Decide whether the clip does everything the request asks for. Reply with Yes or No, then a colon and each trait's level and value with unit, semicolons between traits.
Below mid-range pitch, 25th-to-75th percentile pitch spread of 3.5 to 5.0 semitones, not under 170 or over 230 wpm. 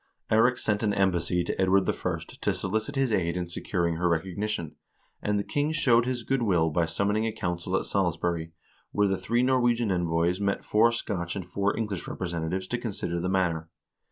Yes: very low, 95 Hz; average, 4.1 semitones; average, 185 wpm